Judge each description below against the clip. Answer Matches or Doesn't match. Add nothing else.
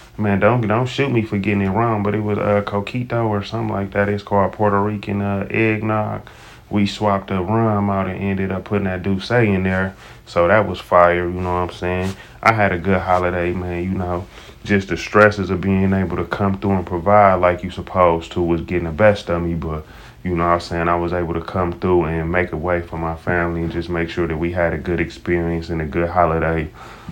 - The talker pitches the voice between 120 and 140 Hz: Doesn't match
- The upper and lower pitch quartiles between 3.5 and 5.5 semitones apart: Doesn't match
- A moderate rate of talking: Doesn't match